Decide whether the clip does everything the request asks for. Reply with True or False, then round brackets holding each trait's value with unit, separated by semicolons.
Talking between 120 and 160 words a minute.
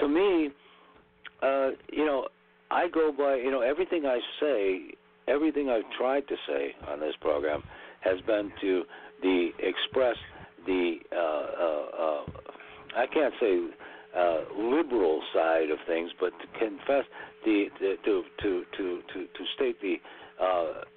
True (145 wpm)